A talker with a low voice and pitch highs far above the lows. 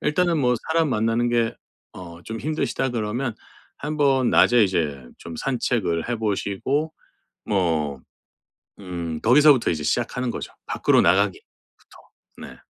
Yes: low, 115 Hz; wide, 7.0 semitones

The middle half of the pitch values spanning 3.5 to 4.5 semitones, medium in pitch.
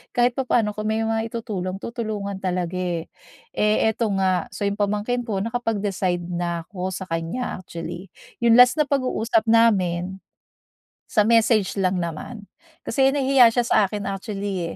No: average, 3.8 semitones; high, 205 Hz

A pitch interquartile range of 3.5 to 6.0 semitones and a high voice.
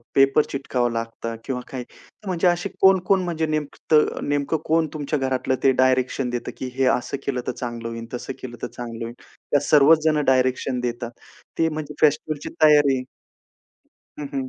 No: average, 3.8 semitones; low, 135 Hz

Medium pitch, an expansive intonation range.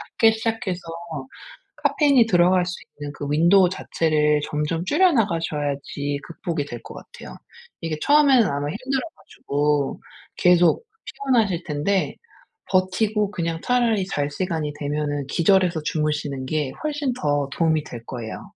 Yes: medium, 170 Hz; wide, 6.0 semitones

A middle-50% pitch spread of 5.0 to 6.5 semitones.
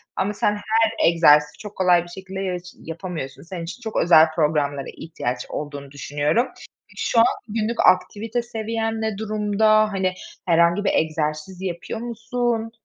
Yes: wide, 5.4 semitones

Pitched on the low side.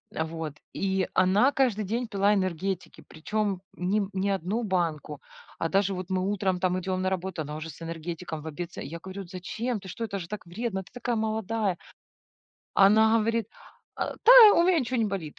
No: high, 190 Hz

